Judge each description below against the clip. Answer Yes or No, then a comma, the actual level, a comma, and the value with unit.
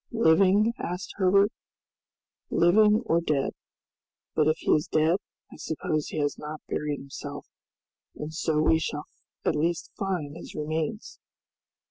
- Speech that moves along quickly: No, slow, 135 wpm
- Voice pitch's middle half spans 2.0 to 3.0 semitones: No, average, 3.6 semitones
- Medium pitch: Yes, medium, 160 Hz